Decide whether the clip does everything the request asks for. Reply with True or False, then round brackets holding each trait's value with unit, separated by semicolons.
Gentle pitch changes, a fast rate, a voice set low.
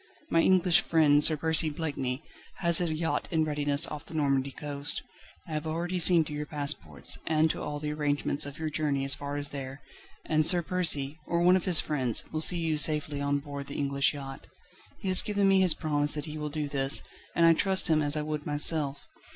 False (2.2 semitones; 215 wpm; 150 Hz)